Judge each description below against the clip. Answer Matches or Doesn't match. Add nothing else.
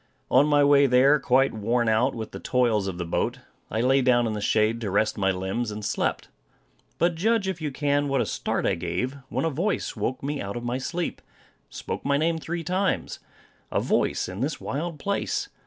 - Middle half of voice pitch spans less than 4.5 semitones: Doesn't match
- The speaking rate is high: Matches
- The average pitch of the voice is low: Matches